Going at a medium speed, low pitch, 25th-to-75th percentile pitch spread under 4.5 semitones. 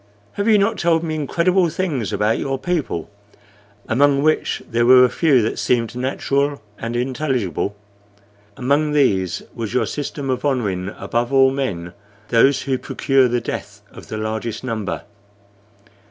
Yes: average, 150 wpm; low, 130 Hz; average, 4.0 semitones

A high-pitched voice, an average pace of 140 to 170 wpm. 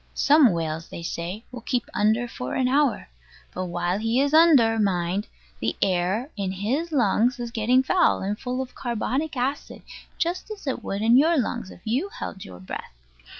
No: high, 235 Hz; average, 185 wpm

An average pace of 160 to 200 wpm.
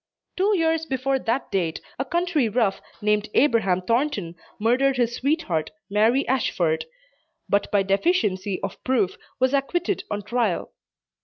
No: slow, 135 wpm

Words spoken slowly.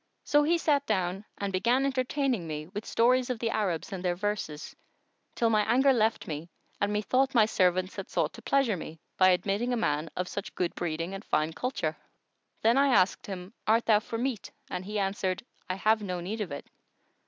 No: average, 200 wpm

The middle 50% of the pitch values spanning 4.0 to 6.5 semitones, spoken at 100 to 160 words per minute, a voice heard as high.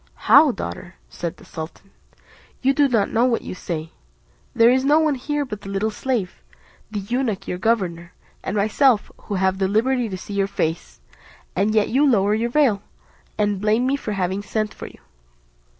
No: average, 4.6 semitones; average, 185 wpm; high, 210 Hz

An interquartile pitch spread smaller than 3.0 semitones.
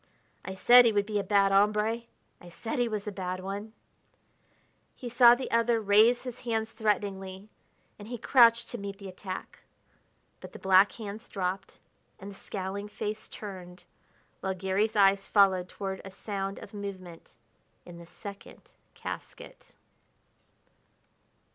Yes: narrow, 2.5 semitones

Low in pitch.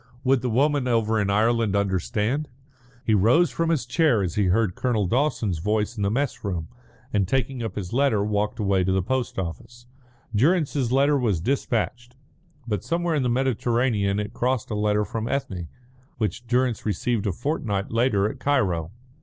Yes: low, 115 Hz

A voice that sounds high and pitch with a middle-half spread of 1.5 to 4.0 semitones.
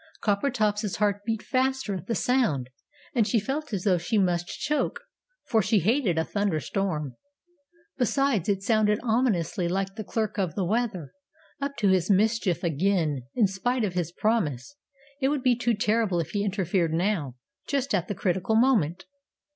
No: high, 205 Hz; average, 4.6 semitones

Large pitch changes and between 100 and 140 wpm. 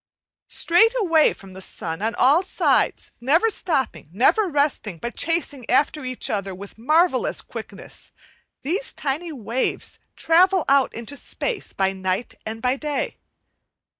Yes: wide, 7.0 semitones; slow, 135 wpm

